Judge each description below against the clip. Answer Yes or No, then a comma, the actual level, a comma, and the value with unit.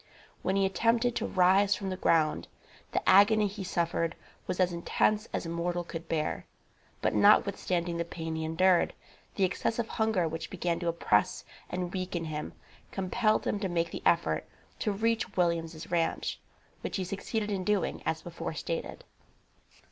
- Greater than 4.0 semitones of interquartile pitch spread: No, average, 3.1 semitones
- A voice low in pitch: No, medium, 180 Hz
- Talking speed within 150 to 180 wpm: Yes, average, 160 wpm